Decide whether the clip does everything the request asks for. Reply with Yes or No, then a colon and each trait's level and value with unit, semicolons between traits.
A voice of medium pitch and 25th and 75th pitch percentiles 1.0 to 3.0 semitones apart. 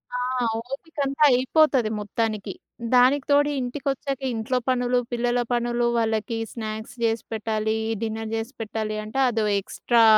No: high, 235 Hz; narrow, 2.6 semitones